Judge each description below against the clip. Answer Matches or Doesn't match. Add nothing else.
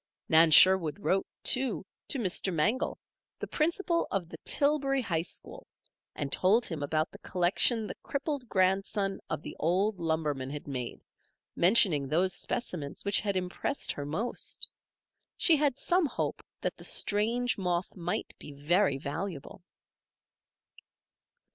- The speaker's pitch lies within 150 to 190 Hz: Matches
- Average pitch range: Doesn't match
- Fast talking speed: Doesn't match